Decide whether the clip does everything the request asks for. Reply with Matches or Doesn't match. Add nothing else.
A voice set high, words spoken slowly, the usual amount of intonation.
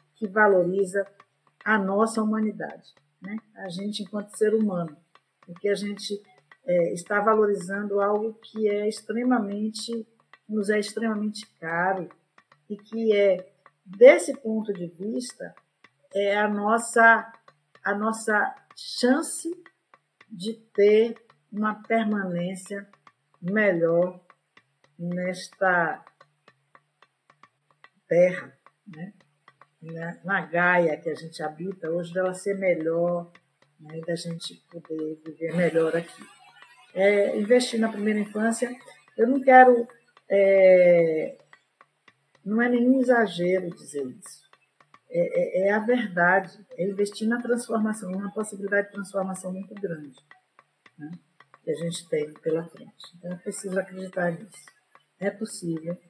Matches